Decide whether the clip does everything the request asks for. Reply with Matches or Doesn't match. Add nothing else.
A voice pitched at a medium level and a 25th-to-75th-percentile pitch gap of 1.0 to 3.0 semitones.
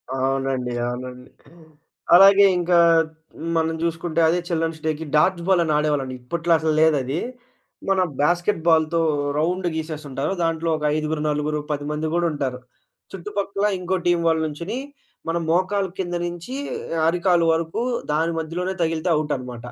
Matches